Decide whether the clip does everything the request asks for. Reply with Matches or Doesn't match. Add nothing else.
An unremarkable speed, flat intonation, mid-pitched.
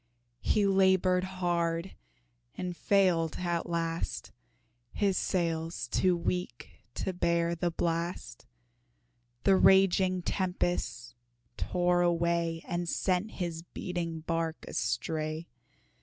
Doesn't match